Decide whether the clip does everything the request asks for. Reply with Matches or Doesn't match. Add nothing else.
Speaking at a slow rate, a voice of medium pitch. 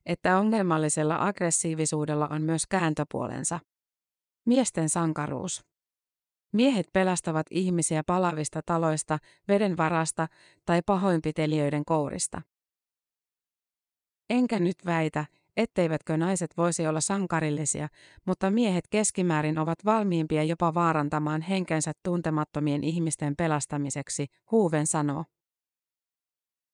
Matches